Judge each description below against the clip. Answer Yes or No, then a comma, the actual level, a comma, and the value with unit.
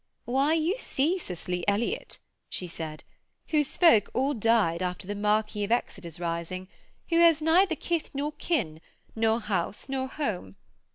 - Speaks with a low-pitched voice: No, high, 225 Hz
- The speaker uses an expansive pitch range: Yes, wide, 8.9 semitones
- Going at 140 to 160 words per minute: Yes, average, 150 wpm